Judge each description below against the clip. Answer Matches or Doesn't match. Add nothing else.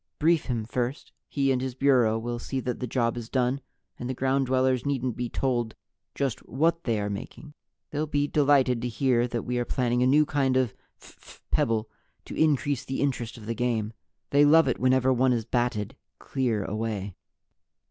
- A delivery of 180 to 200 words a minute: Matches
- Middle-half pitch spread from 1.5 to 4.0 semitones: Matches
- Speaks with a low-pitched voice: Matches